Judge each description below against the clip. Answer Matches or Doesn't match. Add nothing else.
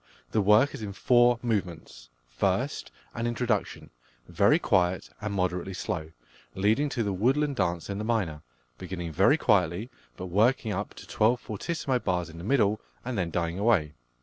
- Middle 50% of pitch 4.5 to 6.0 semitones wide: Matches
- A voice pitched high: Doesn't match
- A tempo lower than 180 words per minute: Matches